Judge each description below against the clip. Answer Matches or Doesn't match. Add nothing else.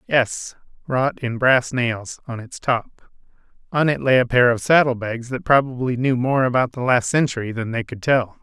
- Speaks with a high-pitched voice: Doesn't match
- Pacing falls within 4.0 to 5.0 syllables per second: Matches